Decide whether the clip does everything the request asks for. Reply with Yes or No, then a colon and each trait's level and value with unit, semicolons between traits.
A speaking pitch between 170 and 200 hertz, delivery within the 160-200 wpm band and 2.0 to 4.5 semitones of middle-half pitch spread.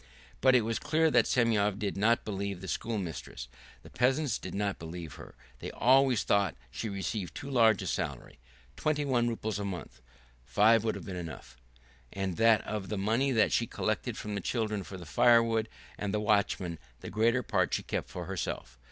No: low, 105 Hz; average, 190 wpm; average, 3.4 semitones